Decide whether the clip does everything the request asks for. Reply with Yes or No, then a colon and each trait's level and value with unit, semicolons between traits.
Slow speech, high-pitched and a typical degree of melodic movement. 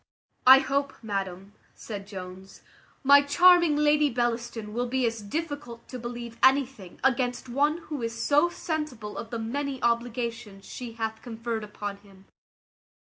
No: average, 145 wpm; high, 240 Hz; average, 4.2 semitones